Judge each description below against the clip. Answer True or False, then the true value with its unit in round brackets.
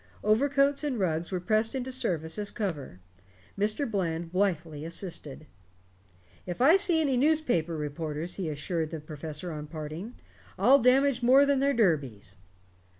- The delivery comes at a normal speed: True (145 wpm)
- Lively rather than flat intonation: True (8.3 semitones)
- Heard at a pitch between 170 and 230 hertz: True (185 Hz)